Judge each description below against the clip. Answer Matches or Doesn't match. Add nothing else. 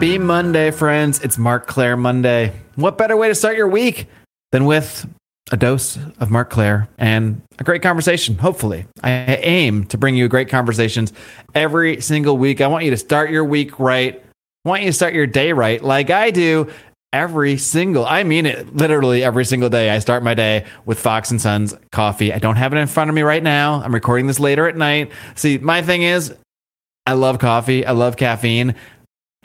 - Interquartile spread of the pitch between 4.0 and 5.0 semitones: Matches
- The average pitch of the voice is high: Doesn't match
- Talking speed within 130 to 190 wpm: Doesn't match